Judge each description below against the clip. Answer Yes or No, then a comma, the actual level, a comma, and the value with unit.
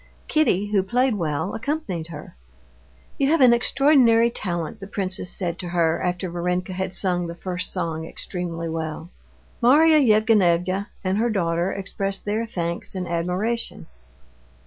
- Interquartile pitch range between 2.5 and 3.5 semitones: No, average, 4.6 semitones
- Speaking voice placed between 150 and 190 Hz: Yes, medium, 185 Hz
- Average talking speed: Yes, average, 145 wpm